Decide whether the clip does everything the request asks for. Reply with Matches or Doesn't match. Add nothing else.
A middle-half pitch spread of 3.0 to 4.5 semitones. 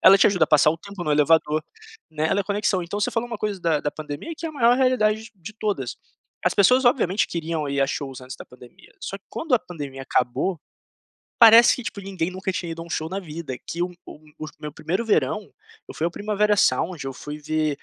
Doesn't match